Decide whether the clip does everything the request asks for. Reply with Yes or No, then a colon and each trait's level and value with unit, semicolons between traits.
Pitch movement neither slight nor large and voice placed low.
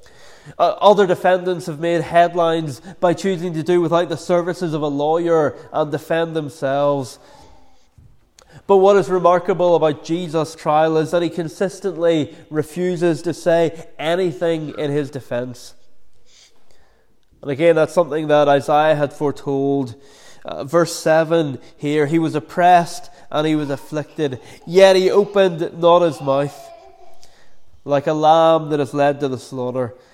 No: average, 3.1 semitones; medium, 160 Hz